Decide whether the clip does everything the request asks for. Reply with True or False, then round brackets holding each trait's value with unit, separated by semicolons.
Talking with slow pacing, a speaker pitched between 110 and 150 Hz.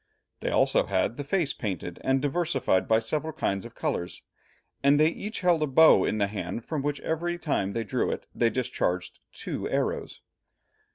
False (180 wpm; 135 Hz)